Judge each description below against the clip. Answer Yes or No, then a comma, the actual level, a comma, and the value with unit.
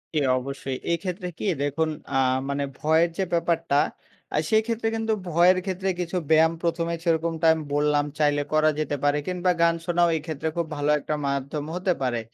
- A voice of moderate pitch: Yes, medium, 160 Hz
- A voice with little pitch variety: No, average, 3.2 semitones